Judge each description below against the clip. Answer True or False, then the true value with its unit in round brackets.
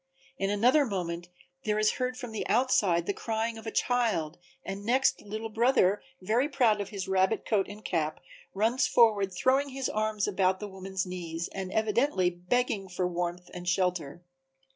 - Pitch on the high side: True (205 Hz)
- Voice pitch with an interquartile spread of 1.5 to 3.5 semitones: False (4.0 semitones)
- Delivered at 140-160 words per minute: False (170 wpm)